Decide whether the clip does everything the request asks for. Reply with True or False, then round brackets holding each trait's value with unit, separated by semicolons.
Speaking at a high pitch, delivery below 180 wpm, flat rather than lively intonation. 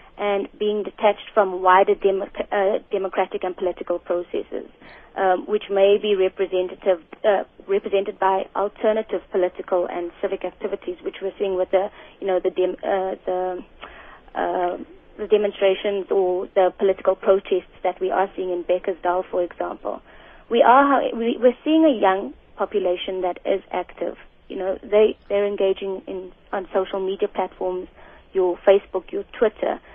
True (195 Hz; 150 wpm; 1.8 semitones)